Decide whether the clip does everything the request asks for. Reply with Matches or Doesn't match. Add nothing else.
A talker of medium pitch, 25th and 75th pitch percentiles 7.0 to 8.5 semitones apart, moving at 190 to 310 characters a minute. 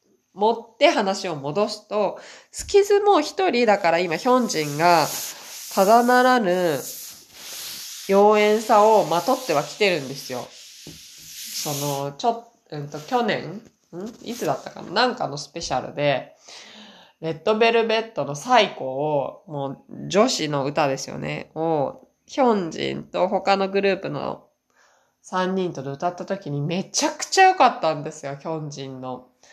Matches